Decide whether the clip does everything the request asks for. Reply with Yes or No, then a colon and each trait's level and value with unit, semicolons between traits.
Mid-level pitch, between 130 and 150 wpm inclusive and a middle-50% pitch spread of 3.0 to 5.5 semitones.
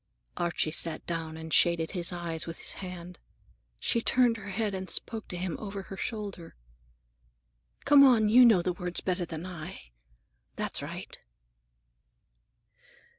Yes: medium, 180 Hz; average, 145 wpm; average, 3.7 semitones